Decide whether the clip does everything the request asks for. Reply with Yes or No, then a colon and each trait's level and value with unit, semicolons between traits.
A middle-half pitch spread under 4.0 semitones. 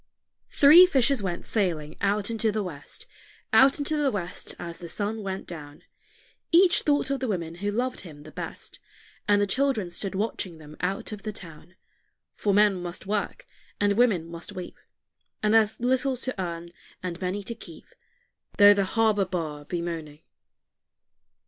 No: average, 4.6 semitones